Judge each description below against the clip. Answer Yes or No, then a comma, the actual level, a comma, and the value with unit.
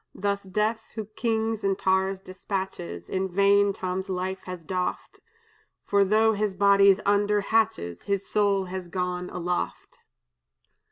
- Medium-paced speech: No, slow, 130 wpm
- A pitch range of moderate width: No, narrow, 1.7 semitones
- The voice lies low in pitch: No, high, 195 Hz